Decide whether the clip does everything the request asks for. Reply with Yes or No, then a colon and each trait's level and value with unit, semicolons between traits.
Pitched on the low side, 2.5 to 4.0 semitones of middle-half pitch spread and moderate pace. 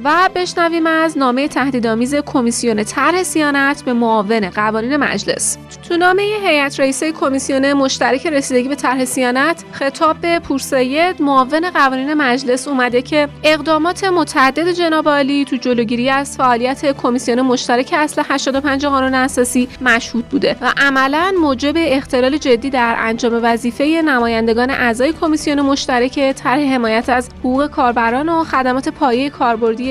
No: very high, 275 Hz; average, 3.4 semitones; average, 130 wpm